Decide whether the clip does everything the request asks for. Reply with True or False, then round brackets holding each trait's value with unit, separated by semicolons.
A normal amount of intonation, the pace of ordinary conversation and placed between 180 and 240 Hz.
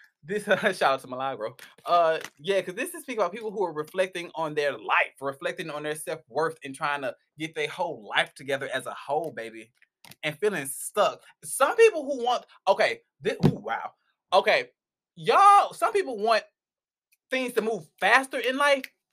False (8.7 semitones; 180 wpm; 185 Hz)